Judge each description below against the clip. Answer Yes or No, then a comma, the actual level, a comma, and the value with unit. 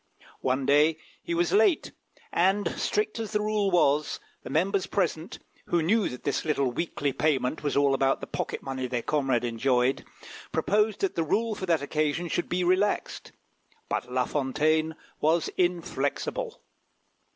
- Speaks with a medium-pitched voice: Yes, medium, 160 Hz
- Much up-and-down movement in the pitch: Yes, wide, 6.1 semitones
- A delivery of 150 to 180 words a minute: Yes, average, 155 wpm